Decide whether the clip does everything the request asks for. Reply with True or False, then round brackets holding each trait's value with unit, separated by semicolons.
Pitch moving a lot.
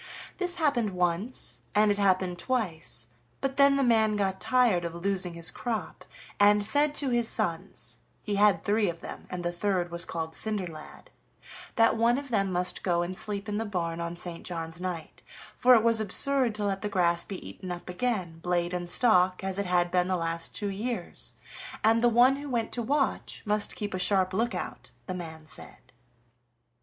False (4.5 semitones)